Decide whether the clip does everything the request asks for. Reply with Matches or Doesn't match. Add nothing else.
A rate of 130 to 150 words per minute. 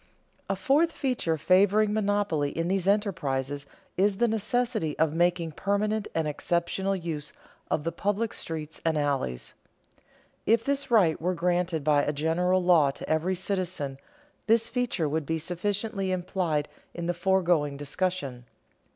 Matches